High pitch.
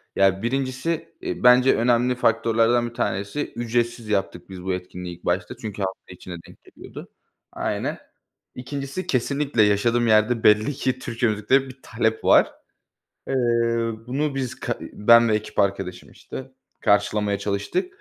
No: low, 115 Hz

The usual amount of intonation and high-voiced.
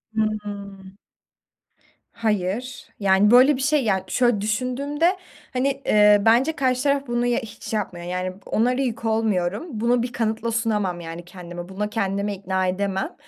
Yes: average, 4.1 semitones; high, 220 Hz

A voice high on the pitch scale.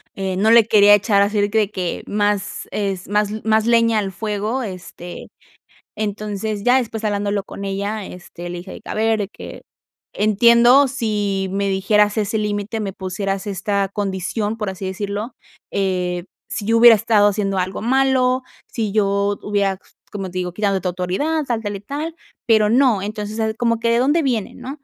Yes: high, 205 Hz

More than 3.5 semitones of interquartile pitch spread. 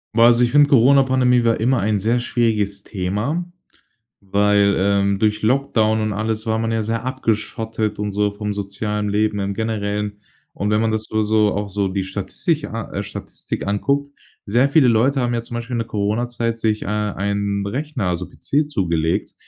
No: average, 2.8 semitones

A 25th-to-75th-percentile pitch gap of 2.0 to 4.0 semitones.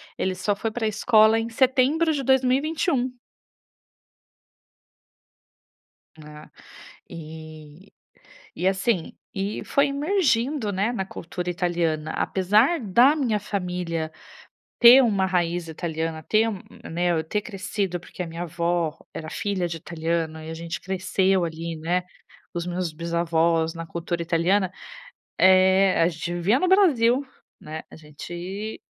No: average, 4.9 semitones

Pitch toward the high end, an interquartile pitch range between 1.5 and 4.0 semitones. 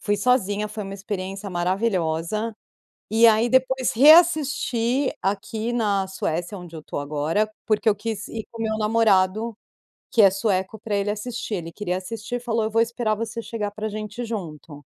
Yes: high, 215 Hz; average, 3.1 semitones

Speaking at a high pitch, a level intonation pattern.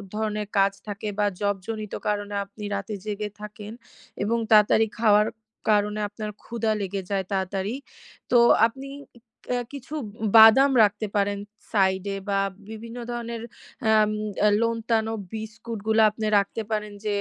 Yes: high, 215 Hz; narrow, 1.7 semitones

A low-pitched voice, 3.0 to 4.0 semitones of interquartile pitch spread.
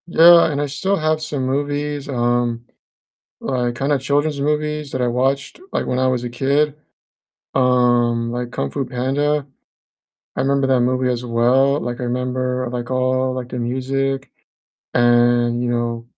No: low, 130 Hz; narrow, 2.5 semitones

